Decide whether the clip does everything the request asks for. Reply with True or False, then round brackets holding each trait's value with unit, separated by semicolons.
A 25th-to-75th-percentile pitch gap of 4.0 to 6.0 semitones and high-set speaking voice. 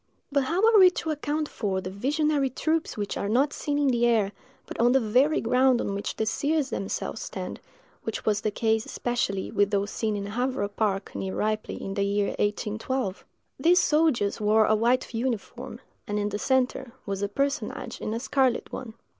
True (4.9 semitones; 230 Hz)